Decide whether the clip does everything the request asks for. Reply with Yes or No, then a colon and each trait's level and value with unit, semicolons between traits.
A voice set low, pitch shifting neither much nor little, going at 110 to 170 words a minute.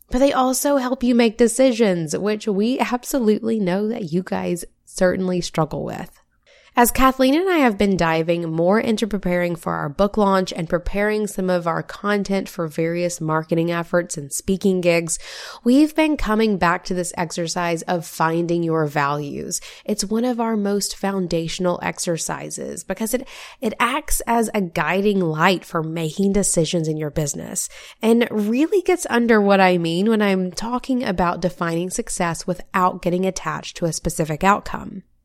No: high, 190 Hz; average, 4.6 semitones; average, 165 wpm